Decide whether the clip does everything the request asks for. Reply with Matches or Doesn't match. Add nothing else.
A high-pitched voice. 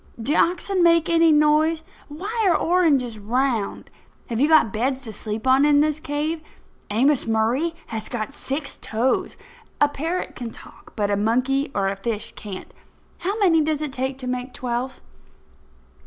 Matches